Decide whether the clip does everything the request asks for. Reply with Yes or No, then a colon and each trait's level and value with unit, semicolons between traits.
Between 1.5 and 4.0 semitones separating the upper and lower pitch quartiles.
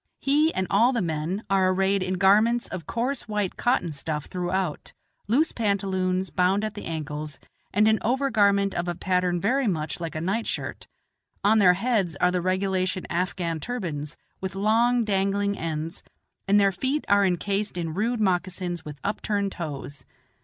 Yes: average, 3.2 semitones